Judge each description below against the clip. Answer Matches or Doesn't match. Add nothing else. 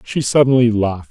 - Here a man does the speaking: Matches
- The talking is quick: Doesn't match